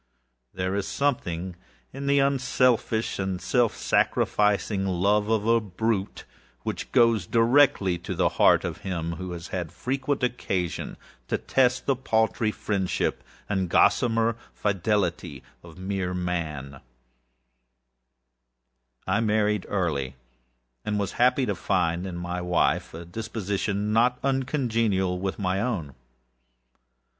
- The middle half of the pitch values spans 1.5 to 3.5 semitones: No, average, 4.5 semitones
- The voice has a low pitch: Yes, low, 100 Hz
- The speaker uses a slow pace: Yes, slow, 120 wpm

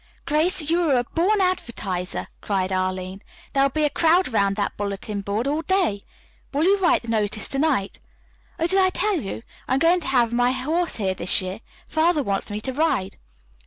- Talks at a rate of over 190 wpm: Yes, average, 200 wpm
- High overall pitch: Yes, very high, 260 Hz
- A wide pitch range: Yes, wide, 8.6 semitones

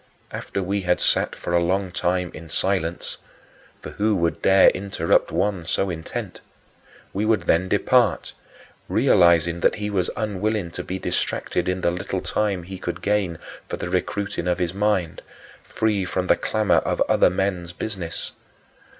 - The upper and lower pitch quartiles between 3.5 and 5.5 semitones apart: No, average, 2.7 semitones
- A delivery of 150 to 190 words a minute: Yes, average, 160 wpm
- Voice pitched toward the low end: Yes, very low, 95 Hz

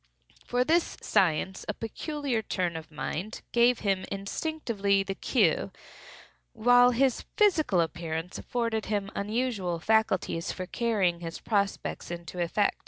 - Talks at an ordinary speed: No, slow, 125 wpm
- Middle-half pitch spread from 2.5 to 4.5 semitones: No, average, 5.1 semitones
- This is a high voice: Yes, high, 200 Hz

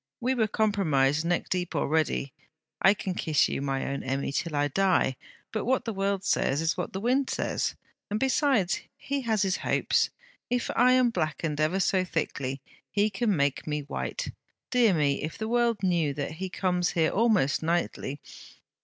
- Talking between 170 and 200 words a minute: Yes, average, 175 wpm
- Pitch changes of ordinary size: No, wide, 6.5 semitones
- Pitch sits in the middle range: Yes, medium, 180 Hz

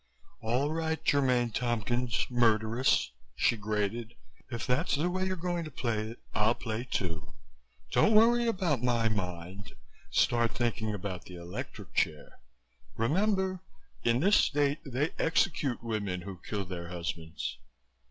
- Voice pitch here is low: Yes, low, 120 Hz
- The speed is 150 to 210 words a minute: No, slow, 135 wpm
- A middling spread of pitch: No, wide, 6.3 semitones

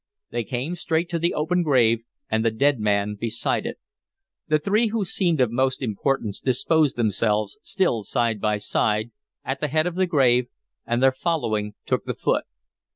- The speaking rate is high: No, average, 175 wpm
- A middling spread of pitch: No, wide, 6.4 semitones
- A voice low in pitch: Yes, low, 130 Hz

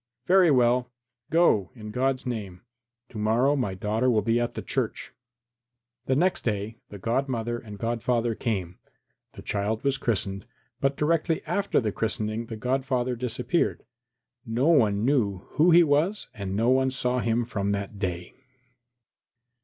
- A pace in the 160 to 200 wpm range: No, average, 150 wpm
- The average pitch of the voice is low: Yes, low, 120 Hz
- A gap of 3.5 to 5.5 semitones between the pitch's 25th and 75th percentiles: Yes, average, 3.9 semitones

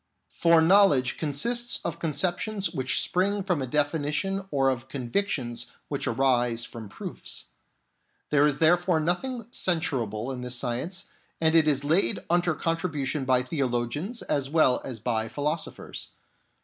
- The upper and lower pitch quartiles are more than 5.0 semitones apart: Yes, wide, 5.4 semitones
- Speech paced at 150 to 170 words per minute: No, slow, 135 wpm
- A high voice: No, medium, 150 Hz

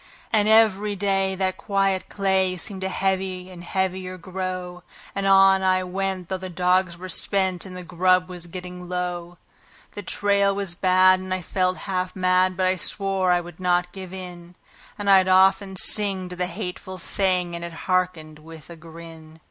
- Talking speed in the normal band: Yes, average, 180 wpm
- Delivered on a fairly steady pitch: Yes, narrow, 1.2 semitones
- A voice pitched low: No, medium, 185 Hz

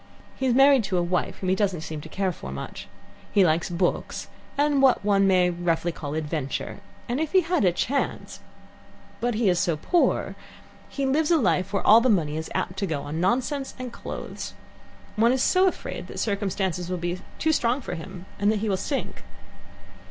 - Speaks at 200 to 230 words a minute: Yes, fast, 205 wpm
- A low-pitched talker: No, high, 195 Hz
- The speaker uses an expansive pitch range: Yes, wide, 6.7 semitones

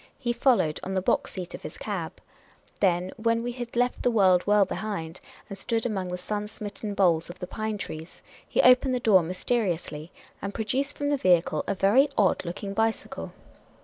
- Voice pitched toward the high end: Yes, high, 205 Hz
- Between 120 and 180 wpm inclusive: No, average, 190 wpm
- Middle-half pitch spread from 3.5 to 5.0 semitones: Yes, average, 4.5 semitones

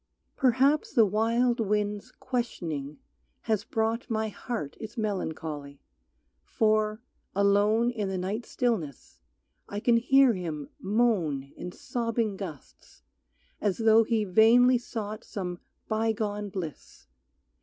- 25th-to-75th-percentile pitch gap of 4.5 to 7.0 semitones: No, average, 3.5 semitones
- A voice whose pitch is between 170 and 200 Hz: No, high, 215 Hz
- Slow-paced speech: Yes, slow, 110 wpm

